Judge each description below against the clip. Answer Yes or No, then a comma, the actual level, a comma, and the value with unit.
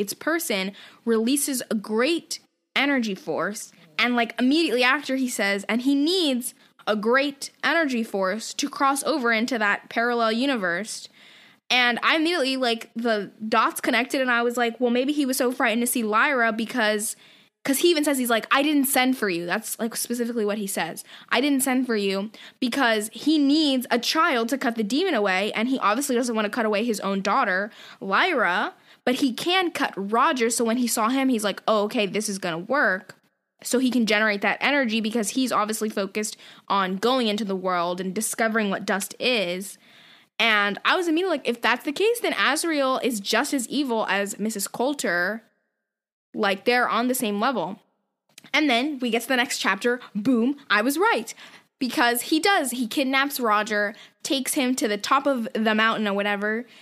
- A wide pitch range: No, average, 4.1 semitones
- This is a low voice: No, high, 235 Hz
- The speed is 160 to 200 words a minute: Yes, average, 190 wpm